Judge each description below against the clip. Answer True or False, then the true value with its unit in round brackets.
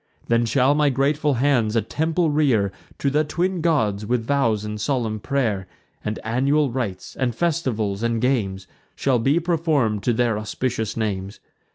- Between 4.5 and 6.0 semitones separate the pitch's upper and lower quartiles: True (5.1 semitones)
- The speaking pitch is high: False (125 Hz)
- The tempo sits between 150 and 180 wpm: True (160 wpm)